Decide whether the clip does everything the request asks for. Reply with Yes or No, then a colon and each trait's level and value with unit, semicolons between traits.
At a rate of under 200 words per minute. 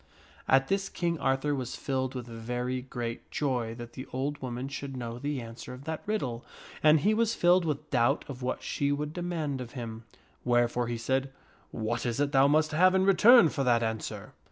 No: fast, 205 wpm